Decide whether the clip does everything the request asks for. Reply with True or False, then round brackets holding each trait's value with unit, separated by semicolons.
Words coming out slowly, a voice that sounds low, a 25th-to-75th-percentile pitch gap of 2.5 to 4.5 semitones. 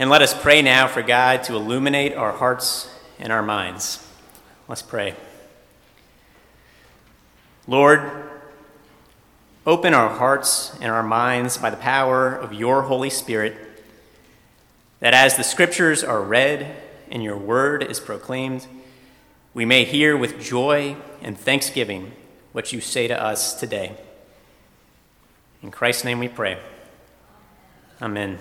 True (125 wpm; 130 Hz; 3.6 semitones)